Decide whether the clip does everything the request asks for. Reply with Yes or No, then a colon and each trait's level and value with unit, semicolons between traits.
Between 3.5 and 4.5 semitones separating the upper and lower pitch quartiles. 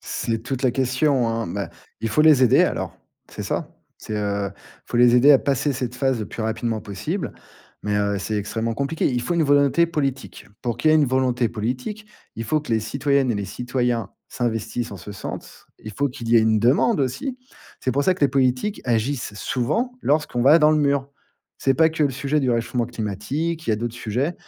Yes: average, 4.0 semitones